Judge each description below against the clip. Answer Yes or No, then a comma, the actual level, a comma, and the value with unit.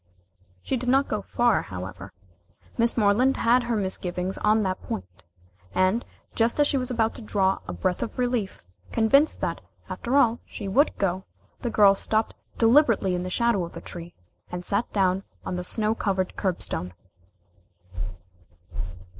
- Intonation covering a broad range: No, average, 4.3 semitones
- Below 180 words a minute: Yes, average, 160 wpm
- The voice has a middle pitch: No, high, 210 Hz